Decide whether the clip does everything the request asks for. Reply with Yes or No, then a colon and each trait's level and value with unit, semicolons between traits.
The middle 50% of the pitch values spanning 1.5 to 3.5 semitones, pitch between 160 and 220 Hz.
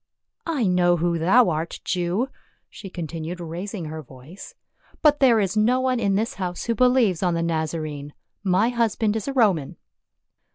No: wide, 5.5 semitones; medium, 185 Hz